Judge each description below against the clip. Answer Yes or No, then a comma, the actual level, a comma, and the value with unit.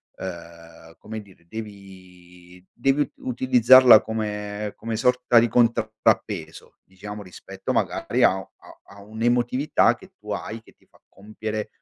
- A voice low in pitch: Yes, low, 105 Hz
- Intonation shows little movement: No, average, 3.7 semitones